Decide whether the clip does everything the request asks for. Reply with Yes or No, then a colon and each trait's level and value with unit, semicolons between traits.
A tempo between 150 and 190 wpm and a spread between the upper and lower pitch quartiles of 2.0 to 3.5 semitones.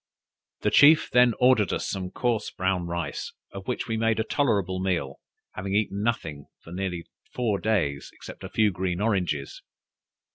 No: average, 160 wpm; average, 4.1 semitones